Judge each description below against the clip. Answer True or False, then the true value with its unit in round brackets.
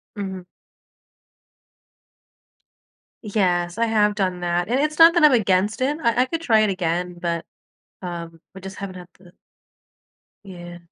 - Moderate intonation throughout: True (4.1 semitones)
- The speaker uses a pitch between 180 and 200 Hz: True (190 Hz)